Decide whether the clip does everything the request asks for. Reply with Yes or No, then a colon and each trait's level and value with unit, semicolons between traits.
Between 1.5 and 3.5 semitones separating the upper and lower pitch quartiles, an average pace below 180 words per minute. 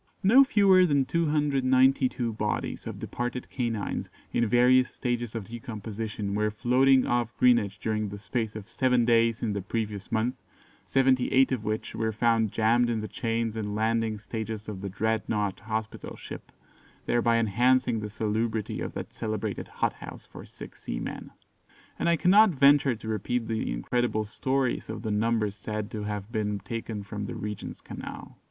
Yes: average, 2.8 semitones; average, 160 wpm